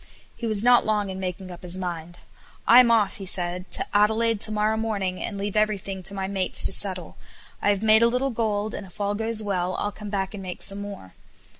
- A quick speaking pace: Yes, fast, 230 wpm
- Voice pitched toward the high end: Yes, high, 205 Hz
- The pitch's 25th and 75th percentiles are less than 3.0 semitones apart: Yes, narrow, 2.6 semitones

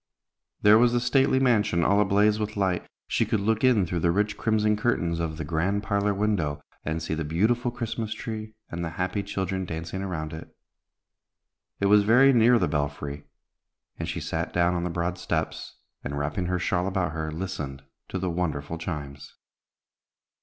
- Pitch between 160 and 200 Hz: No, very low, 90 Hz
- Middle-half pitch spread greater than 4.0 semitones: Yes, average, 4.6 semitones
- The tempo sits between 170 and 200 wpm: Yes, average, 180 wpm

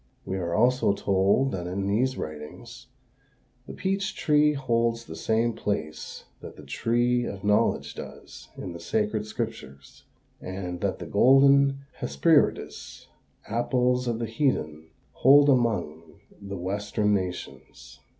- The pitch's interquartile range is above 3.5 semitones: Yes, wide, 5.6 semitones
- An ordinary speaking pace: No, slow, 130 wpm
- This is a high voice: No, low, 110 Hz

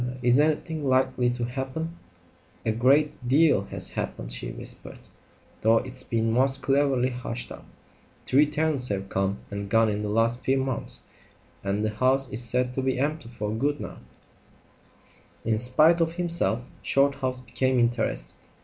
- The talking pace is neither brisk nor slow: Yes, average, 160 wpm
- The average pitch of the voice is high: No, low, 125 Hz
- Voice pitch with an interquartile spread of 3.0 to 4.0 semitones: Yes, average, 3.5 semitones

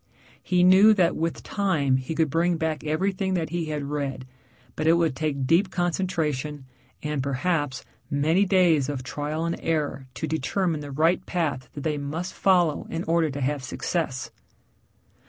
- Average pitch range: Yes, average, 3.4 semitones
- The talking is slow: No, average, 165 wpm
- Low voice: No, medium, 155 Hz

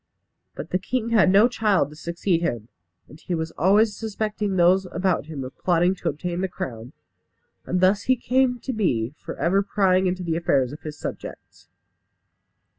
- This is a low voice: No, medium, 180 Hz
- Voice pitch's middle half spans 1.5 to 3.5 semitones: No, average, 4.2 semitones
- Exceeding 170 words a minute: Yes, average, 180 wpm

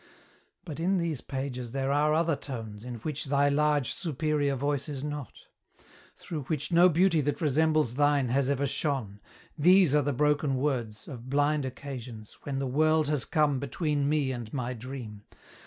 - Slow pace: No, average, 170 wpm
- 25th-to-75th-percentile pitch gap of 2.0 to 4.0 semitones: Yes, average, 2.8 semitones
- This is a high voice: No, medium, 145 Hz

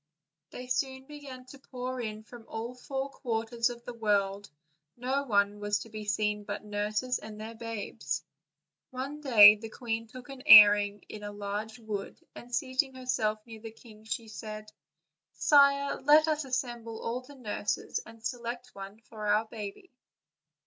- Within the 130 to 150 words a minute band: No, average, 165 wpm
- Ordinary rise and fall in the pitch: Yes, average, 3.2 semitones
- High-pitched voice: Yes, high, 230 Hz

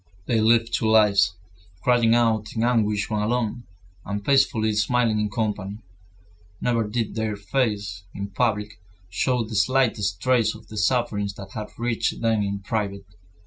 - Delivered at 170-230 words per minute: No, average, 150 wpm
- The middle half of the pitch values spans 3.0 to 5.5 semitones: No, narrow, 2.4 semitones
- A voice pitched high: No, low, 110 Hz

